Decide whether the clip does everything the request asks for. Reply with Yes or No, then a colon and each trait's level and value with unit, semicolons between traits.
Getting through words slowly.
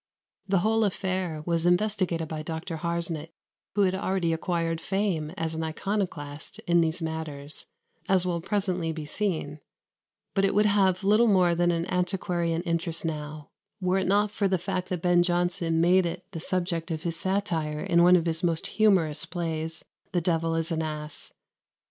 No: average, 175 wpm